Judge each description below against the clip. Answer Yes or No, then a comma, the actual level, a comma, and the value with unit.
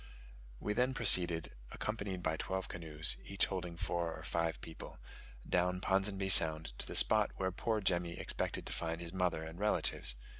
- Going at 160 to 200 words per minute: Yes, average, 165 wpm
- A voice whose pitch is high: No, very low, 90 Hz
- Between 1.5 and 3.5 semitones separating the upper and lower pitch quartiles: Yes, average, 2.8 semitones